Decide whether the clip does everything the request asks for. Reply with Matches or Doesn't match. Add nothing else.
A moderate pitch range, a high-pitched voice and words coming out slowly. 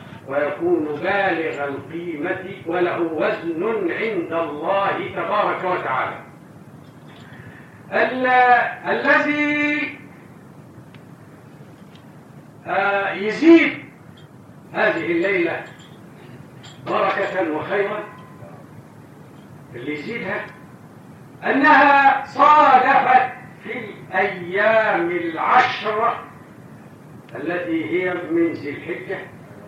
Doesn't match